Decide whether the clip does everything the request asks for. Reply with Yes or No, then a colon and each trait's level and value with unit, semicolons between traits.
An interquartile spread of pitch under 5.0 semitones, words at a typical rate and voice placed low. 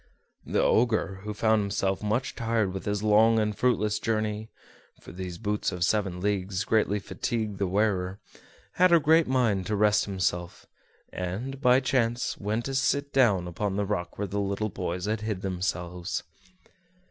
Yes: average, 2.8 semitones; average, 165 wpm; low, 105 Hz